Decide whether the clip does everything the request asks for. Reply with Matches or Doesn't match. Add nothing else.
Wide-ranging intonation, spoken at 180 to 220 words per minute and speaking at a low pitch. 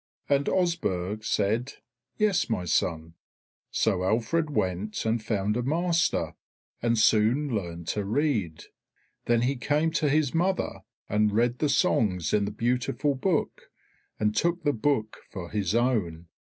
Doesn't match